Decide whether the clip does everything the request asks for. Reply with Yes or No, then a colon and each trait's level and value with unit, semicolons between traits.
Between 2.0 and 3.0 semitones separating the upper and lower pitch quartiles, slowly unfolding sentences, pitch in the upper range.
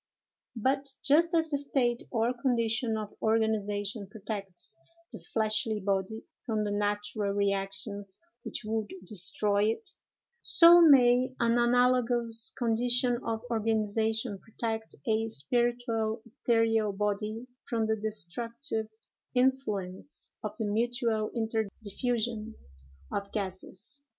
Yes: narrow, 2.5 semitones; slow, 105 wpm; high, 225 Hz